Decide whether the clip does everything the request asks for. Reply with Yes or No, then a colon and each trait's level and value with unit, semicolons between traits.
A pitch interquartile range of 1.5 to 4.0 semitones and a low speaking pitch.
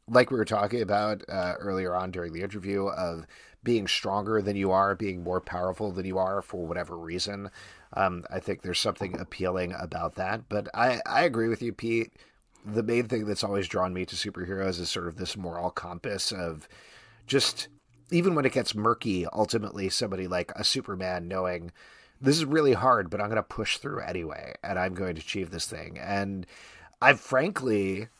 Yes: average, 3.3 semitones; low, 100 Hz